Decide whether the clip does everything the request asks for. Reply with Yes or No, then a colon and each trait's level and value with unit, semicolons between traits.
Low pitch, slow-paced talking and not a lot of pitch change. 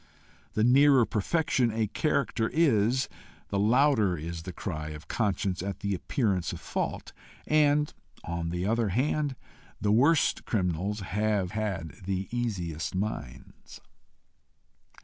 No: low, 105 Hz; slow, 125 wpm; wide, 5.4 semitones